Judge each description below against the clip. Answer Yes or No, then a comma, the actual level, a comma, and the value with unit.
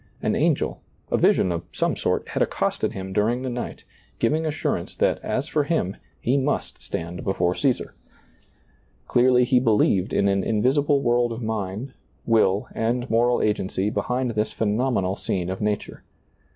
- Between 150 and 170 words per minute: Yes, average, 155 wpm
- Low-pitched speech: Yes, low, 115 Hz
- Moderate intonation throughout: Yes, average, 4.4 semitones